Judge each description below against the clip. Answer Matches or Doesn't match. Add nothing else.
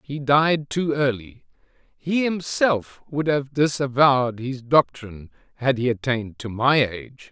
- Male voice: Matches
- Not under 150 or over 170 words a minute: Doesn't match